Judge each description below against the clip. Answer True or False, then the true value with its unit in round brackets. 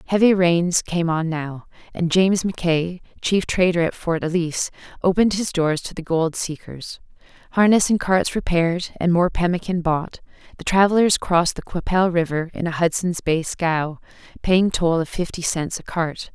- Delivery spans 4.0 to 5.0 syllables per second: True (4.9 syllables/s)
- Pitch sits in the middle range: True (175 Hz)